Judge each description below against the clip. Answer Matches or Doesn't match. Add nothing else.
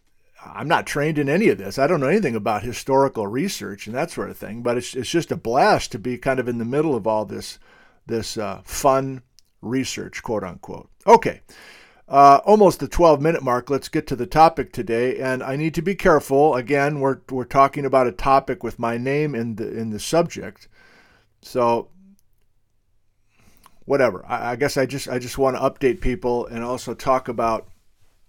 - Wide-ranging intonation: Doesn't match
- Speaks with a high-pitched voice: Doesn't match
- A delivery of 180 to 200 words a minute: Matches